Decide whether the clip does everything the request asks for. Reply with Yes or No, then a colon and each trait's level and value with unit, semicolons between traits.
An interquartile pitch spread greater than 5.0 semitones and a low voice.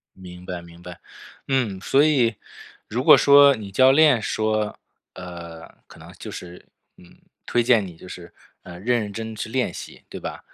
Yes: wide, 5.6 semitones; low, 105 Hz